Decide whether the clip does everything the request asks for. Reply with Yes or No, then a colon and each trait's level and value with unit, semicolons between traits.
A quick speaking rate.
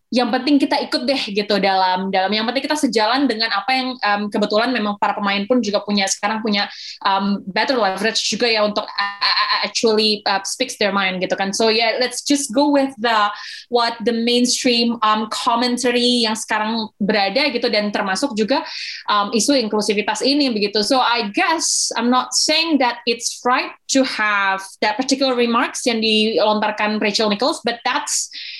Yes: fast, 175 wpm